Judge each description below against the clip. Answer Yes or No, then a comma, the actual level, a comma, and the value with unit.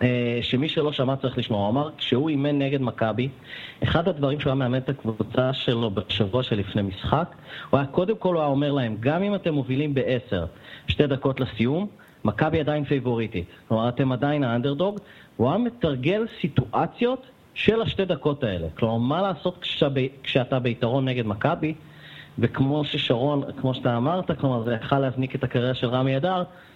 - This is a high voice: No, low, 135 Hz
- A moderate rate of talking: No, fast, 170 wpm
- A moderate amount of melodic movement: Yes, average, 3.6 semitones